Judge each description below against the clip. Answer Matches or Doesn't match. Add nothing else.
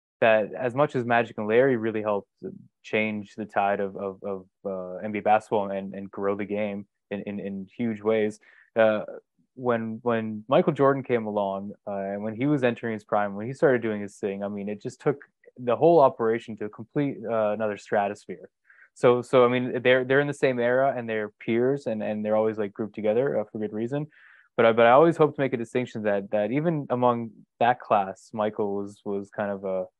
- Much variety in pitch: Doesn't match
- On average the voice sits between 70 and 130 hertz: Matches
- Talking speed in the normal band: Doesn't match